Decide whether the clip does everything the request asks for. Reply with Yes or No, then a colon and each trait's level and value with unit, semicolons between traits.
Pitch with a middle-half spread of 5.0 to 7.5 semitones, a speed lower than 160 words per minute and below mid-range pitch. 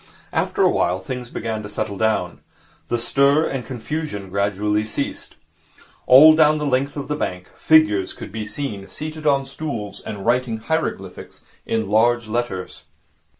Yes: average, 5.3 semitones; average, 150 wpm; low, 120 Hz